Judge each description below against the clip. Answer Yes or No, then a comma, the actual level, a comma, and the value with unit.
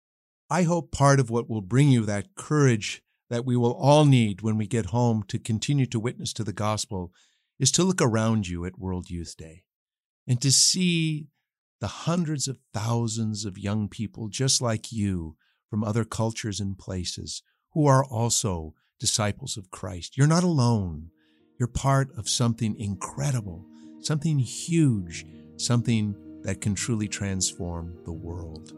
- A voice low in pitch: Yes, low, 110 Hz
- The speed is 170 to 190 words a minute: No, average, 160 wpm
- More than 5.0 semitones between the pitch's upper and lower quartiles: Yes, wide, 5.5 semitones